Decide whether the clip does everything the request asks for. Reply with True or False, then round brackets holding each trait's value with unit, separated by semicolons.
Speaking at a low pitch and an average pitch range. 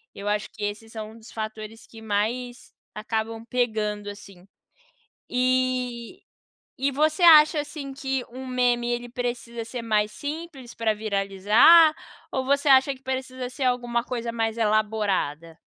False (235 Hz; 3.2 semitones)